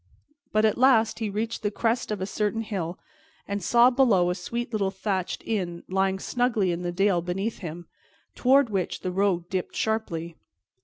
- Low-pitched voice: No, high, 200 Hz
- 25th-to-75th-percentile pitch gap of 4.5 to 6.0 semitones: No, average, 3.8 semitones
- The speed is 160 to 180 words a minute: Yes, average, 175 wpm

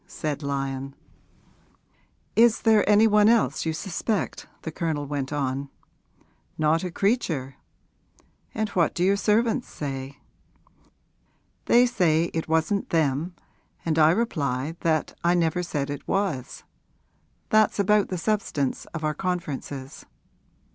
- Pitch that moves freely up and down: Yes, wide, 6.0 semitones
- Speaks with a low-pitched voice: No, medium, 165 Hz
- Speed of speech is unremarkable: No, slow, 125 wpm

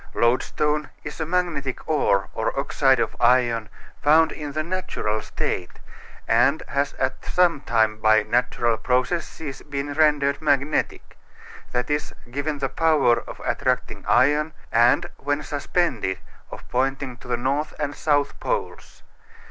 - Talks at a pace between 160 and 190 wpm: No, slow, 135 wpm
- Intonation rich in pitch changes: No, average, 3.6 semitones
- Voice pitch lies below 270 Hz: Yes, medium, 140 Hz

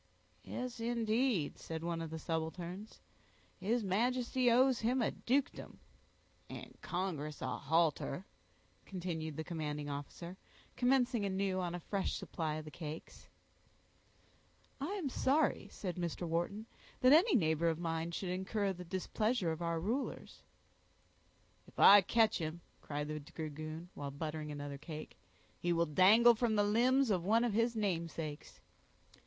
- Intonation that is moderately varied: No, wide, 6.1 semitones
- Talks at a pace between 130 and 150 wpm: Yes, average, 145 wpm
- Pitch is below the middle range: No, medium, 180 Hz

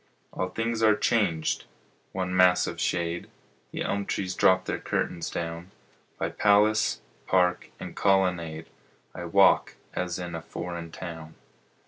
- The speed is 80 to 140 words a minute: Yes, slow, 135 wpm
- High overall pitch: No, very low, 90 Hz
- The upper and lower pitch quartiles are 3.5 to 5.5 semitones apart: No, narrow, 2.6 semitones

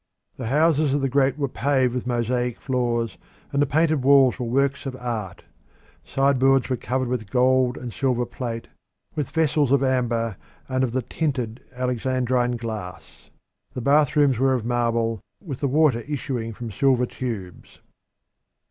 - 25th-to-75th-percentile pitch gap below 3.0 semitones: Yes, narrow, 2.4 semitones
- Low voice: Yes, low, 125 Hz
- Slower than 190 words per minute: Yes, average, 155 wpm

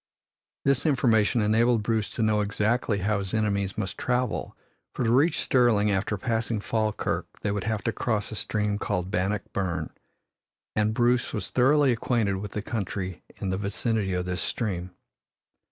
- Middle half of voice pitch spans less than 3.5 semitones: Yes, average, 2.8 semitones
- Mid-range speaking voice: No, low, 105 Hz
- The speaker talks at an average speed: Yes, average, 165 wpm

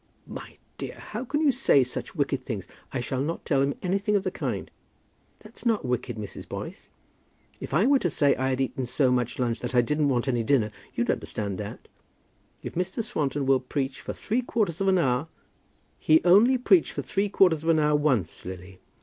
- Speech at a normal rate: No, fast, 210 wpm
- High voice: No, medium, 140 Hz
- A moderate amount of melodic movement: No, wide, 7.0 semitones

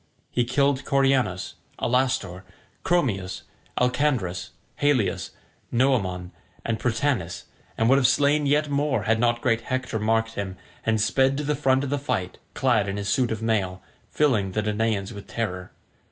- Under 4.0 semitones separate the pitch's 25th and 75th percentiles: No, average, 4.8 semitones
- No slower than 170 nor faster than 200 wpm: No, average, 155 wpm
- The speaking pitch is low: Yes, low, 120 Hz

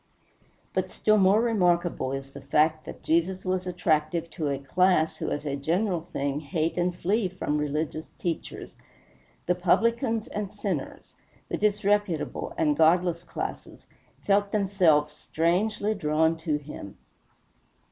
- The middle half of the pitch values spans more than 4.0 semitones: Yes, average, 4.4 semitones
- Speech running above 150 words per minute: No, slow, 135 wpm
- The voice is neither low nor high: Yes, medium, 170 Hz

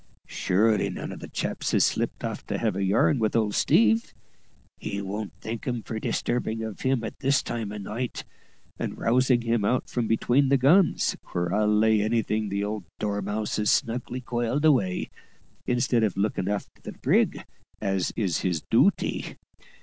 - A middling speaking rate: Yes, average, 175 wpm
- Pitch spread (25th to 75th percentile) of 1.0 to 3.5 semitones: Yes, average, 2.8 semitones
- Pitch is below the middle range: Yes, low, 110 Hz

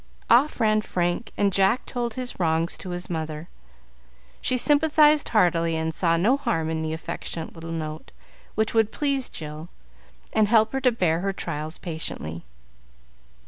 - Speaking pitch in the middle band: Yes, medium, 180 Hz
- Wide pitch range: Yes, wide, 6.5 semitones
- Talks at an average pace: Yes, average, 155 wpm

